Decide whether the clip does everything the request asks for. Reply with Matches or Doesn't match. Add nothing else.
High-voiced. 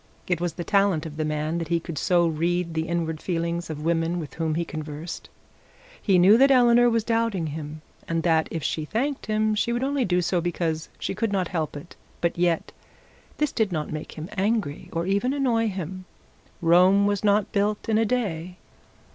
Doesn't match